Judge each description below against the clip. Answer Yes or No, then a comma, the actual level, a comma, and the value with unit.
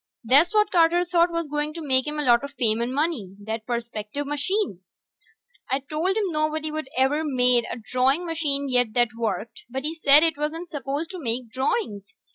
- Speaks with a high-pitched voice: Yes, very high, 280 Hz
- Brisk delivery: No, average, 190 wpm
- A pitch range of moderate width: Yes, average, 4.9 semitones